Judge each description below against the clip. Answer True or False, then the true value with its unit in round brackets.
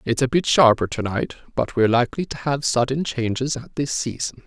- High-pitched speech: False (130 Hz)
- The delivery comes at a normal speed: False (215 wpm)